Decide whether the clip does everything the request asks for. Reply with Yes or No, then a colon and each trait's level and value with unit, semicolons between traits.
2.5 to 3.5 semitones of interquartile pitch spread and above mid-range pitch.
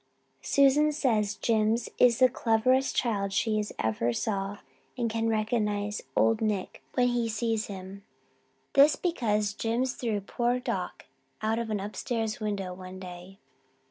Yes: average, 2.9 semitones; high, 220 Hz